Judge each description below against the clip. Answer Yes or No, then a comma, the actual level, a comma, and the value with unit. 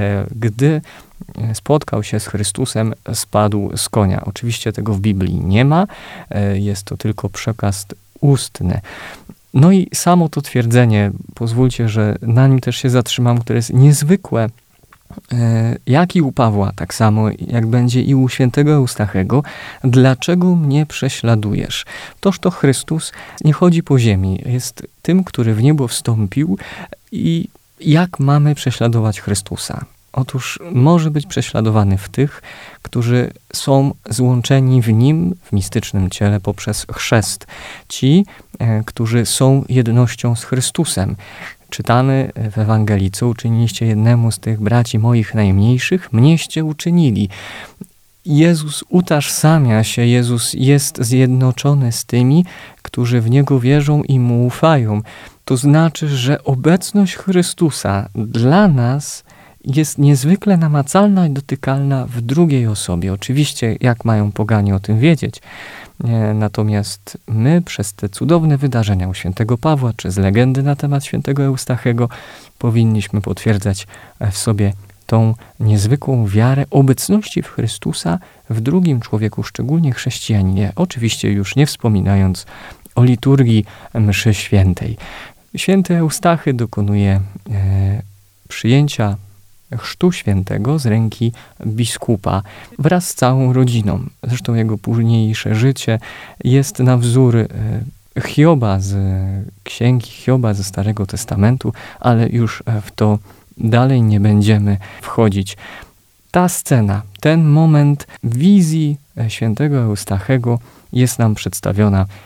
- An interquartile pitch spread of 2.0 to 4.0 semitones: No, average, 4.9 semitones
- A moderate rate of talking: Yes, average, 120 wpm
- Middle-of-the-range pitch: No, low, 120 Hz